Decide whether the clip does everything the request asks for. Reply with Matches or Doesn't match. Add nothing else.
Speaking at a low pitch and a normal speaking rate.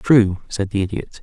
Matches